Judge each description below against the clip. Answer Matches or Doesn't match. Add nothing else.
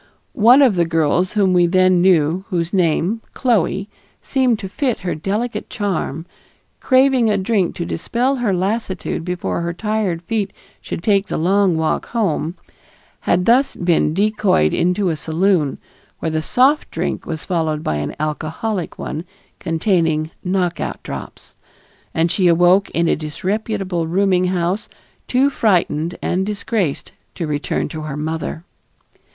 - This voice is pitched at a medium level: Matches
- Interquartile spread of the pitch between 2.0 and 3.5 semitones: Doesn't match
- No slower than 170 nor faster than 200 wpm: Doesn't match